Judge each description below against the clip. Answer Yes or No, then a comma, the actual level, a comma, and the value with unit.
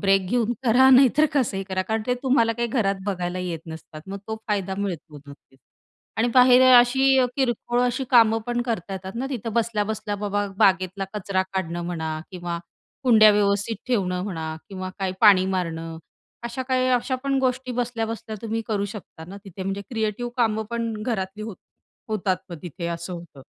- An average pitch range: Yes, average, 4.3 semitones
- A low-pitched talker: No, high, 210 Hz